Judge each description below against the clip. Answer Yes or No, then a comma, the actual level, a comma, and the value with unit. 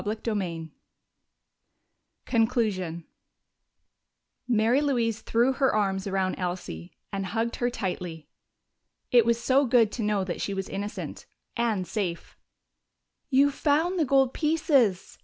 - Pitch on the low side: No, high, 220 Hz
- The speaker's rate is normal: No, slow, 120 wpm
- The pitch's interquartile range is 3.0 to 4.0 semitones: No, average, 4.9 semitones